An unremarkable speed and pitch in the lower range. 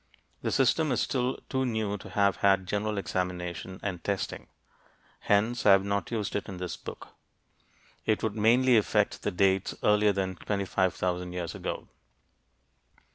Yes: average, 150 wpm; low, 100 Hz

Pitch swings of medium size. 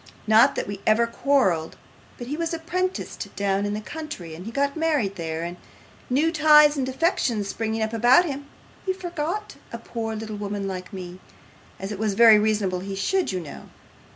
No: wide, 7.2 semitones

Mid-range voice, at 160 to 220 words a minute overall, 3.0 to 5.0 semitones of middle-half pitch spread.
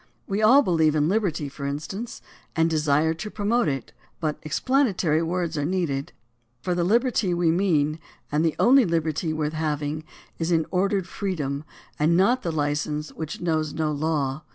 Yes: medium, 160 Hz; average, 165 wpm; average, 3.7 semitones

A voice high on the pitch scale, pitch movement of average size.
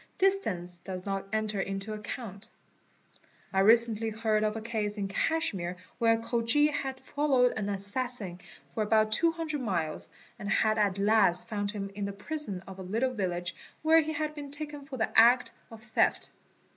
Yes: high, 220 Hz; average, 4.6 semitones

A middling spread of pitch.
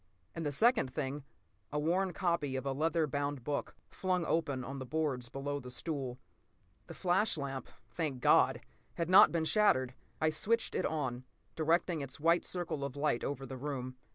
Yes: average, 3.8 semitones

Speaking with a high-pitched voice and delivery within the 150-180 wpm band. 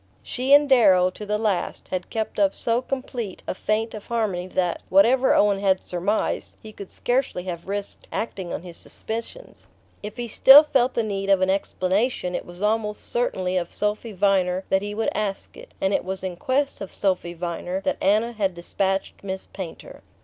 No: high, 200 Hz; average, 190 wpm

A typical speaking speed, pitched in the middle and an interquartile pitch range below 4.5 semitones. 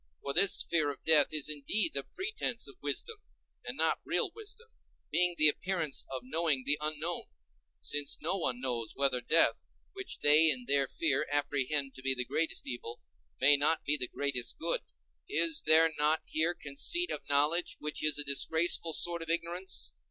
Yes: average, 175 wpm; medium, 150 Hz; average, 3.2 semitones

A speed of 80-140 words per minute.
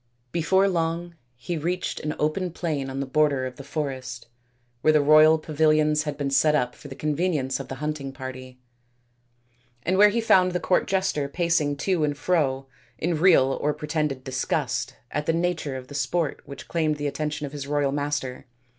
No: average, 185 wpm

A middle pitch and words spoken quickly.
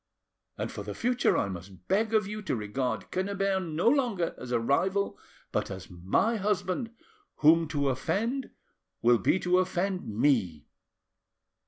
No: medium, 175 Hz; average, 150 wpm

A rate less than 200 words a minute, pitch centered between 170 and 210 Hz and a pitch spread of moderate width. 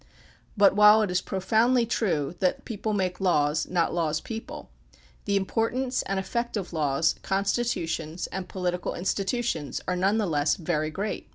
Yes: average, 160 wpm; high, 190 Hz; average, 4.3 semitones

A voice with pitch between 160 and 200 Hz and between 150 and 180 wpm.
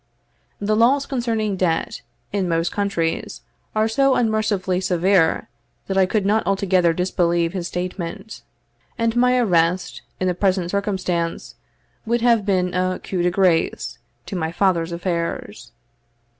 No: medium, 185 Hz; slow, 135 wpm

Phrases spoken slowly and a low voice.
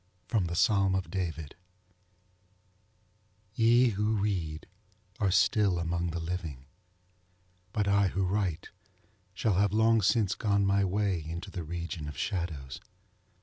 Yes: slow, 125 wpm; very low, 95 Hz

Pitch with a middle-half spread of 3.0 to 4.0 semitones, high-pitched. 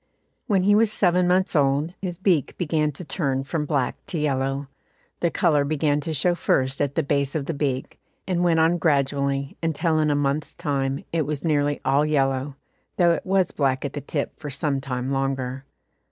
No: average, 3.3 semitones; medium, 145 Hz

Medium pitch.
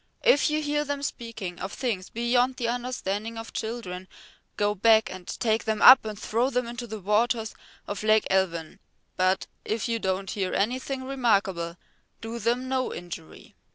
No: high, 225 Hz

